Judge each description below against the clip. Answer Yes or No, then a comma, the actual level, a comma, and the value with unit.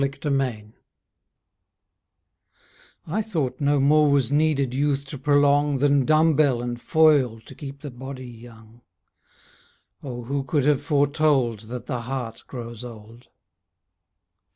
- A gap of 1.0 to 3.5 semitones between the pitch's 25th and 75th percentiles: Yes, average, 3.1 semitones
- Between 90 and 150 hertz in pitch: Yes, low, 135 Hz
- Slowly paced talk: Yes, slow, 130 wpm